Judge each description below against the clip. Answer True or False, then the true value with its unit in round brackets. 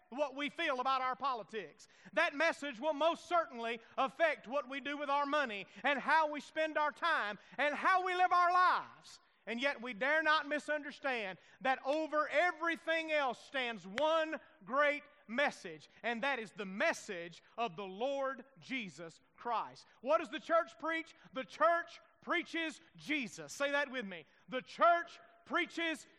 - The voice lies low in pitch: False (290 Hz)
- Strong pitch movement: False (4.2 semitones)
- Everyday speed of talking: True (165 wpm)